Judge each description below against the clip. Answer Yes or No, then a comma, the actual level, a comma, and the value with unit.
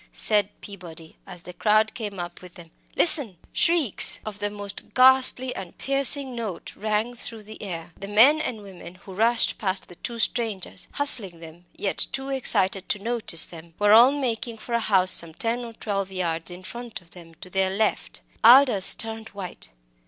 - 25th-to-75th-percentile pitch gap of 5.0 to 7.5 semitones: No, average, 4.4 semitones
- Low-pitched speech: No, high, 210 Hz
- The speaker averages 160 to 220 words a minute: Yes, average, 185 wpm